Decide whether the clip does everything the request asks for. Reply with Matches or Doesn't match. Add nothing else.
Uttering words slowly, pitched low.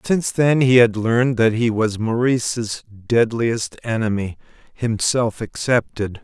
Matches